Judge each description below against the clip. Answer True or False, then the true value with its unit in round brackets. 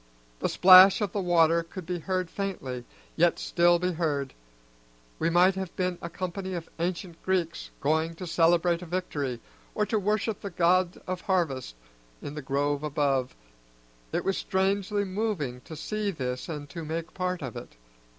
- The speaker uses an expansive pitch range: False (3.2 semitones)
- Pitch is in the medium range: True (175 Hz)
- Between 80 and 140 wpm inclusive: False (170 wpm)